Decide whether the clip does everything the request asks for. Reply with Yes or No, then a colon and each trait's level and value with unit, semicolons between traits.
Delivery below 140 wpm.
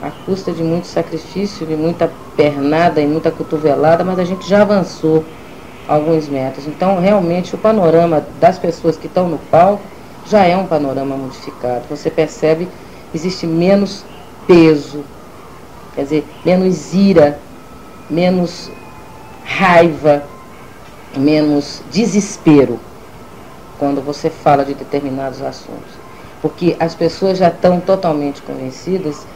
Yes: slow, 120 wpm